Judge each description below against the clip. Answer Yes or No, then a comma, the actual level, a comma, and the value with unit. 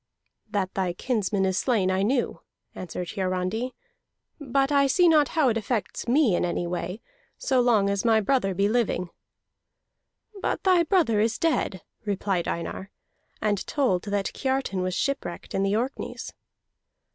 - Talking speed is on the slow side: No, average, 150 wpm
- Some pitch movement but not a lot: No, wide, 5.8 semitones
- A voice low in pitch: No, high, 210 Hz